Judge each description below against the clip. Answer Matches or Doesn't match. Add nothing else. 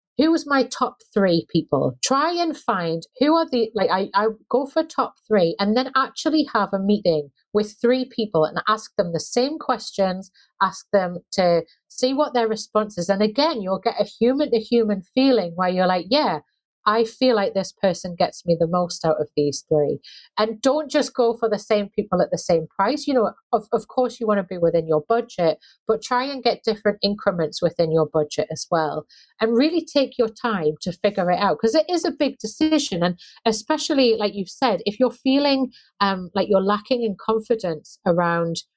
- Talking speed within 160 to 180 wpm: Doesn't match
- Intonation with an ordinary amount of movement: Doesn't match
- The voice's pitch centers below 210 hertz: Doesn't match